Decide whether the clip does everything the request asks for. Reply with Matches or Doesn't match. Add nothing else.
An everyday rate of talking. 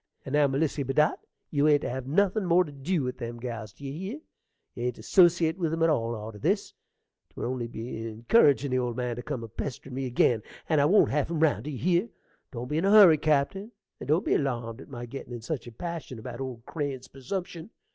Doesn't match